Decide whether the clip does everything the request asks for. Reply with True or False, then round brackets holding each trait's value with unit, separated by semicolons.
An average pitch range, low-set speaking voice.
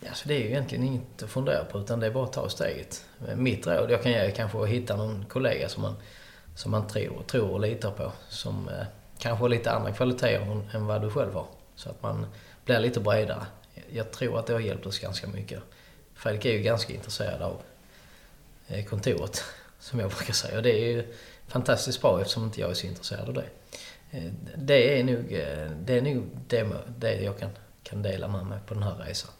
True (3.0 semitones; 110 Hz)